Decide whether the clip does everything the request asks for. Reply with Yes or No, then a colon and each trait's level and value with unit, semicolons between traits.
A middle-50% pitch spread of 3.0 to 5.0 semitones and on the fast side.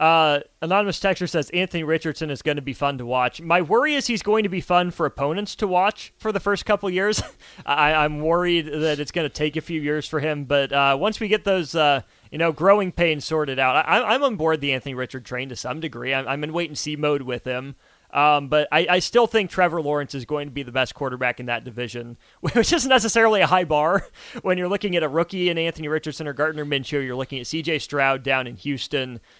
Yes: average, 4.4 semitones; fast, 245 wpm